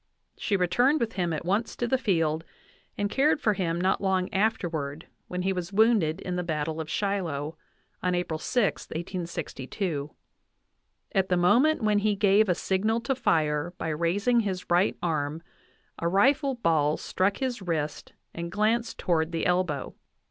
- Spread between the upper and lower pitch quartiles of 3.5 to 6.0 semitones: Yes, average, 4.4 semitones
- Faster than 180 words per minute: No, average, 165 wpm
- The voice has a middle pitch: Yes, medium, 180 Hz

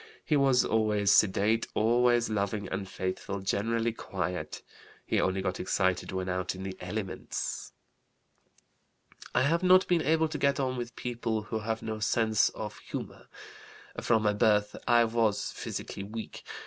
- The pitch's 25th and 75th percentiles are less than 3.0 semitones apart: No, average, 3.3 semitones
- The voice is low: Yes, low, 110 Hz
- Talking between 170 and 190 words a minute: No, average, 150 wpm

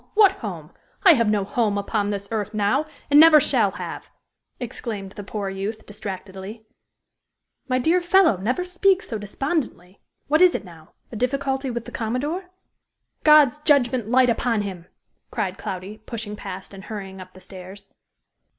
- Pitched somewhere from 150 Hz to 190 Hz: No, high, 220 Hz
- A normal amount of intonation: No, wide, 5.7 semitones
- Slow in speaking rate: No, average, 160 wpm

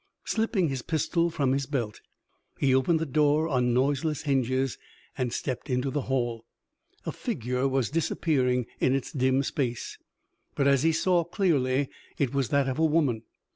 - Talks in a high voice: No, low, 135 Hz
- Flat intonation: No, average, 3.2 semitones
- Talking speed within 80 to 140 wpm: No, average, 165 wpm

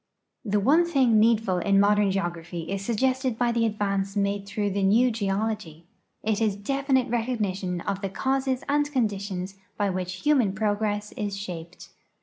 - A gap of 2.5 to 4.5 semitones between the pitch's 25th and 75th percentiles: Yes, average, 3.4 semitones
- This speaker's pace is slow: No, average, 155 wpm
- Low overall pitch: No, high, 205 Hz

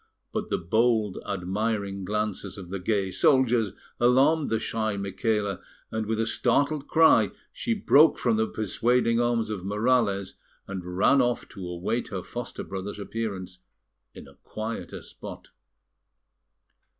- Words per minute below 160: Yes, average, 140 wpm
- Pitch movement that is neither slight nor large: Yes, average, 3.5 semitones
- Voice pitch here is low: Yes, low, 110 Hz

